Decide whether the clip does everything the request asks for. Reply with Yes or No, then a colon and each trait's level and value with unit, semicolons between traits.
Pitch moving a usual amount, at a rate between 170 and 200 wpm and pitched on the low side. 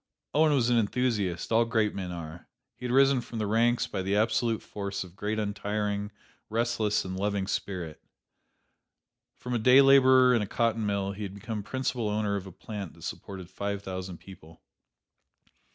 Yes: average, 3.2 semitones; average, 180 wpm; low, 105 Hz